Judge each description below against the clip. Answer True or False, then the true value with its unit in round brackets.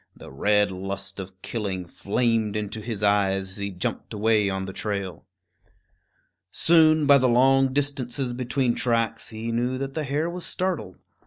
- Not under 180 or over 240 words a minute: False (160 wpm)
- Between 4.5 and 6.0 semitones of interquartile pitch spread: True (5.0 semitones)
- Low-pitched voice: True (110 Hz)